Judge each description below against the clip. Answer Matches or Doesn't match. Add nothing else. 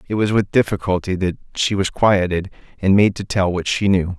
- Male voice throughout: Matches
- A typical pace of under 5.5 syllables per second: Matches